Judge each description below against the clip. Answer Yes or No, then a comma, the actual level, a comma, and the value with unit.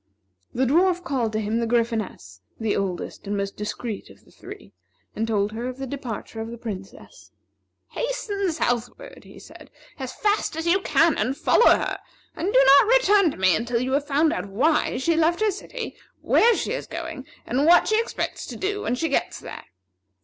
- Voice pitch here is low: No, very high, 270 Hz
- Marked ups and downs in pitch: Yes, wide, 7.3 semitones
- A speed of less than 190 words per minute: No, average, 195 wpm